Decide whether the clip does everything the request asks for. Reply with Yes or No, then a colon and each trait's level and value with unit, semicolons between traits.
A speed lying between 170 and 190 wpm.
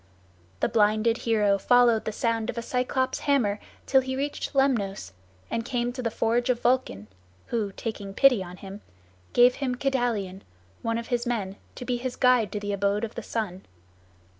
Yes: average, 180 wpm